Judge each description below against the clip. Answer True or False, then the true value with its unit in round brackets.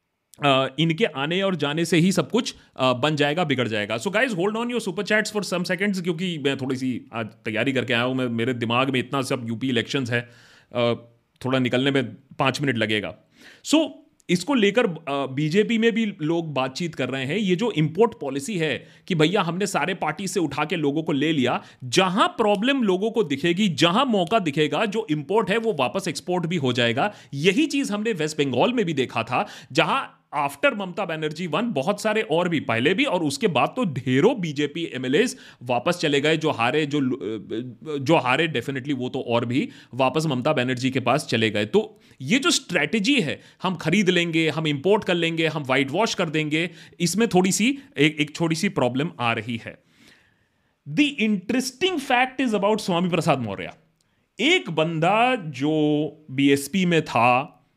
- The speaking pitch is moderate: True (155 Hz)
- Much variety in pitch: True (7.4 semitones)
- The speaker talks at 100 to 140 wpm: False (190 wpm)